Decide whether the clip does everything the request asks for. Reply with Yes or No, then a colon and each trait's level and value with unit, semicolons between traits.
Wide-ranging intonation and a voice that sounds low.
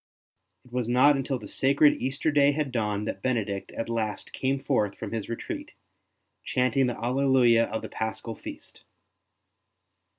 No: average, 3.3 semitones; low, 125 Hz